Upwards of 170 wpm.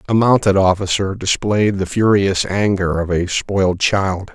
No: average, 150 wpm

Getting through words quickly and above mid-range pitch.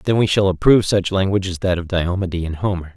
No: fast, 245 wpm; very low, 95 Hz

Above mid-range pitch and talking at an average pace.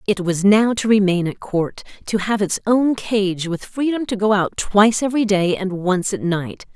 No: high, 200 Hz; fast, 215 wpm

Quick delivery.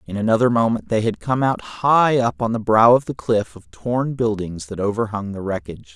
Yes: fast, 220 wpm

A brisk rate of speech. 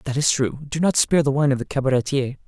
Yes: fast, 265 wpm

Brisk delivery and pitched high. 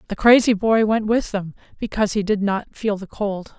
Yes: fast, 220 wpm; high, 210 Hz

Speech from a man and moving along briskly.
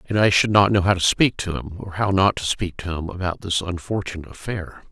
Yes: male; fast, 255 wpm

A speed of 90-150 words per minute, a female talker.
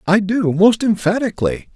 No: slow, 135 wpm; male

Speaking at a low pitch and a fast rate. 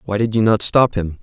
Yes: low, 105 Hz; fast, 295 wpm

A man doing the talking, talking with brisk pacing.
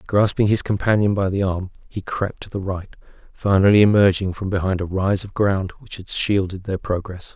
No: male; average, 195 wpm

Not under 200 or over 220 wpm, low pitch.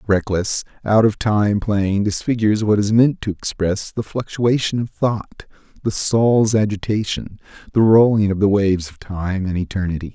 No: average, 160 wpm; low, 105 Hz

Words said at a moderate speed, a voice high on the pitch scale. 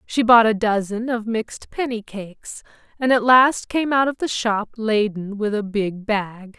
Yes: average, 190 wpm; high, 220 Hz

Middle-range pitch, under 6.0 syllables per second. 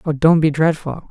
Yes: medium, 155 Hz; 5.4 syllables/s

